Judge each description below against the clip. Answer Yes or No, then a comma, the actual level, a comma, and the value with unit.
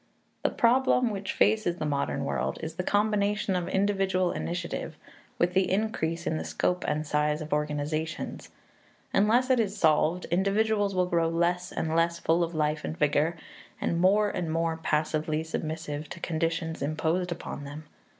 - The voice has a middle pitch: Yes, medium, 170 Hz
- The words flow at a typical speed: Yes, average, 160 wpm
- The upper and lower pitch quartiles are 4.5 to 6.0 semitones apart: No, average, 3.7 semitones